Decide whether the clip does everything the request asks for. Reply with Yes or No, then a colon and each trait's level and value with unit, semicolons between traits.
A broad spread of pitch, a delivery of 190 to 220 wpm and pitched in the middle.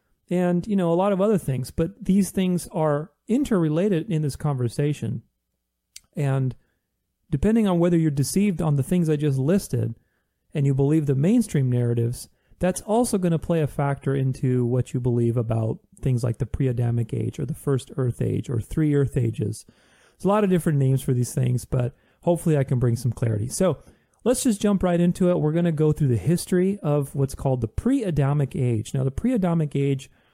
Yes: wide, 5.7 semitones; average, 200 wpm; medium, 145 Hz